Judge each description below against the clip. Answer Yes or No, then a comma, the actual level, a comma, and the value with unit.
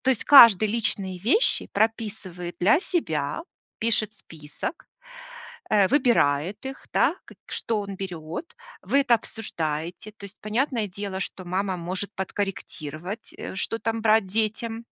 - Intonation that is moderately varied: Yes, average, 3.8 semitones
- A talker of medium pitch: No, high, 205 Hz